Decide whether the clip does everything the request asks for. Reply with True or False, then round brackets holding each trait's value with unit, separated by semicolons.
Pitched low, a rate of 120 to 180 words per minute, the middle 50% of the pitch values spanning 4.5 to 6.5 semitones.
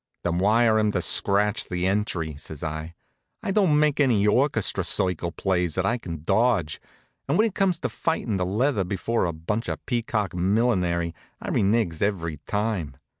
True (100 Hz; 175 wpm; 5.2 semitones)